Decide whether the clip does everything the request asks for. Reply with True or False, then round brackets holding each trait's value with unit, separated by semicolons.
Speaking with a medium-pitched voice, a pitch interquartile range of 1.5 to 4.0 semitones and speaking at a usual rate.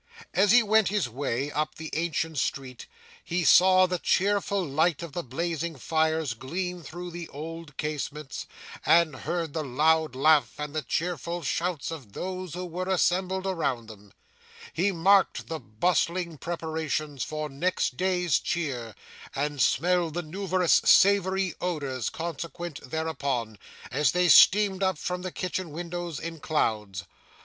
True (165 Hz; 3.5 semitones; 145 wpm)